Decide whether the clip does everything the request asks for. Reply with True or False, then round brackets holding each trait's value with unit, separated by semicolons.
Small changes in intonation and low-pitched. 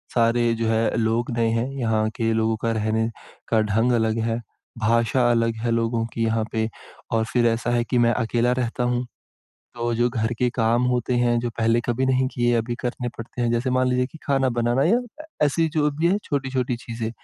True (1.7 semitones; 120 Hz)